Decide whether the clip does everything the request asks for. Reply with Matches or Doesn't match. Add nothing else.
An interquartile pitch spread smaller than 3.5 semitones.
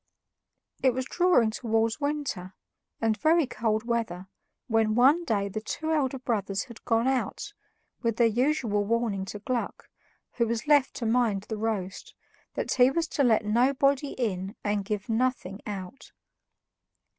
Doesn't match